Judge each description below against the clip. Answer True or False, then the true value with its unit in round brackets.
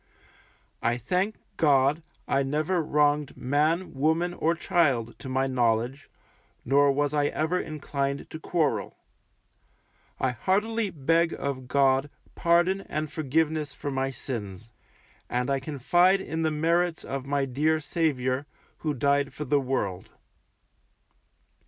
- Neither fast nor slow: False (125 wpm)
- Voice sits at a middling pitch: True (145 Hz)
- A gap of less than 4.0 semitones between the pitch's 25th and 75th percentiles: True (3.4 semitones)